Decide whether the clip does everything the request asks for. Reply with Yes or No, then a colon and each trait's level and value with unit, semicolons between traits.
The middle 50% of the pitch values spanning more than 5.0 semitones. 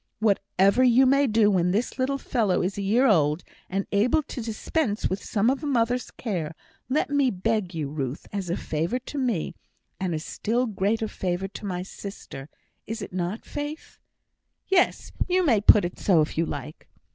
Yes: wide, 5.6 semitones